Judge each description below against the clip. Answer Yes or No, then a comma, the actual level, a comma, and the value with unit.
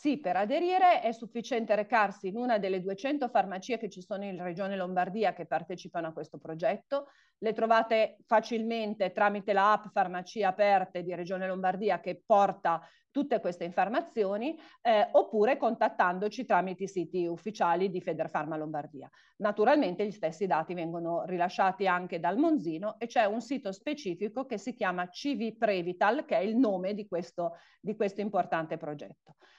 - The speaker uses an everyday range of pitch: Yes, average, 4.1 semitones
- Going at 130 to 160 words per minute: Yes, average, 155 wpm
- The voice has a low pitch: No, high, 200 Hz